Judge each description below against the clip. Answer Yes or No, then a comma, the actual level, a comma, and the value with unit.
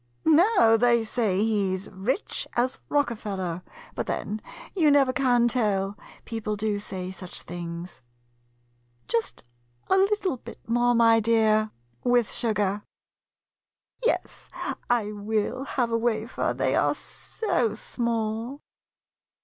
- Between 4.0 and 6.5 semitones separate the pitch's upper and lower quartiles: No, average, 2.9 semitones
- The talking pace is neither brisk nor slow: No, slow, 120 wpm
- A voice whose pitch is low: No, high, 225 Hz